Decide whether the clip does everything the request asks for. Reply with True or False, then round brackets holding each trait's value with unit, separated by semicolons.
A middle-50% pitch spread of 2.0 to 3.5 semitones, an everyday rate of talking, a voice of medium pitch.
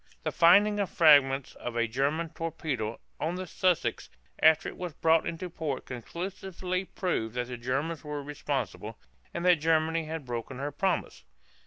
False (4.3 semitones; 160 wpm; 155 Hz)